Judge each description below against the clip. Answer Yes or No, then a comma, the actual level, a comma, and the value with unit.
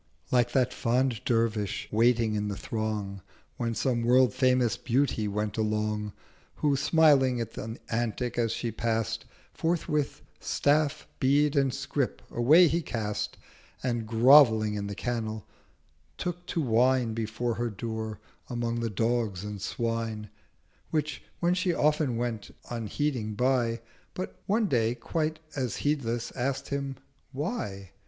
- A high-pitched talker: No, low, 120 Hz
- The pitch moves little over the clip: No, average, 3.7 semitones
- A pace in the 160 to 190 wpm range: No, slow, 135 wpm